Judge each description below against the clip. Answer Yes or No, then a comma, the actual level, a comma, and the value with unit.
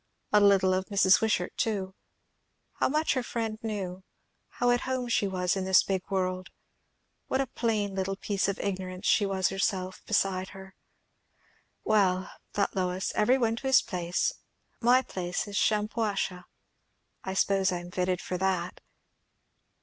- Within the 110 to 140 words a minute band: No, average, 155 wpm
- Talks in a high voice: Yes, high, 195 Hz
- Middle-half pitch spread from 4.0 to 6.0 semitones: No, average, 2.7 semitones